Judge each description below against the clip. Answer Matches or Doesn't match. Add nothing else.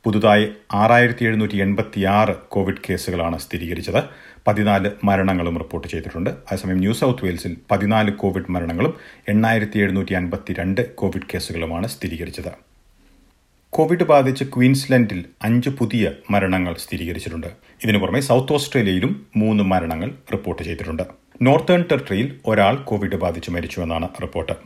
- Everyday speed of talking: Matches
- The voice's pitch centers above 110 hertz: Doesn't match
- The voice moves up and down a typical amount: Matches